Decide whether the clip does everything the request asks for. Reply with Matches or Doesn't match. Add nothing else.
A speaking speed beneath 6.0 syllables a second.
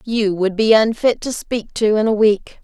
Matches